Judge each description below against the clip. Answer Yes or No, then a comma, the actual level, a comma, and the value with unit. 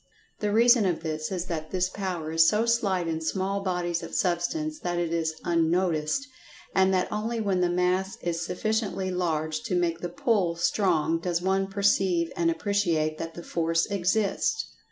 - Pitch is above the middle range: No, medium, 180 Hz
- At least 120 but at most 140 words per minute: No, average, 175 wpm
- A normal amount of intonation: Yes, average, 3.0 semitones